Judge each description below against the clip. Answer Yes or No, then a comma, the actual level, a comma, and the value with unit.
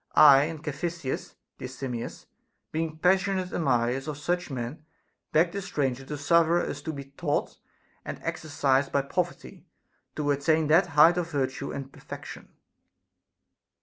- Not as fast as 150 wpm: Yes, average, 140 wpm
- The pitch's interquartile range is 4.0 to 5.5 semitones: No, average, 3.5 semitones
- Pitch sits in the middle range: Yes, medium, 150 Hz